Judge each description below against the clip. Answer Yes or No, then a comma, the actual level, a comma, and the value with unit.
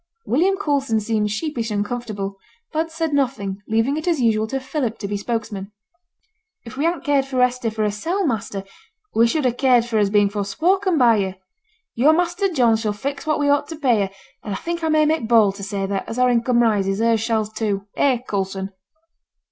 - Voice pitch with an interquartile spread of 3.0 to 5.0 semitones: No, wide, 5.6 semitones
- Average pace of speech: No, fast, 210 wpm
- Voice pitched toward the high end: Yes, high, 235 Hz